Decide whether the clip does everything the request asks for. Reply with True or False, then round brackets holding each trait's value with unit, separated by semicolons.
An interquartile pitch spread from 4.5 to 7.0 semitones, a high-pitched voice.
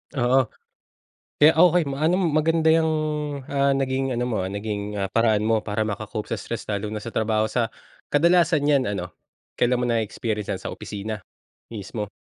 False (4.8 semitones; 115 Hz)